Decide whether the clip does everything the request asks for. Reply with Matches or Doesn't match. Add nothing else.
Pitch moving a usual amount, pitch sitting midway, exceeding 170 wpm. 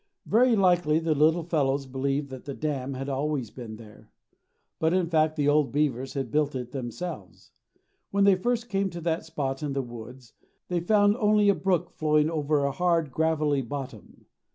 Matches